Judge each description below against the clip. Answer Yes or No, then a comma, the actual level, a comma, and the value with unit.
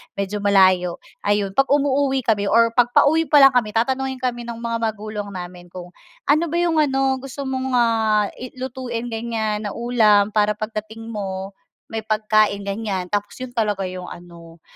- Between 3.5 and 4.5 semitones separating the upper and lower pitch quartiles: Yes, average, 4.0 semitones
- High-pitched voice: Yes, high, 220 Hz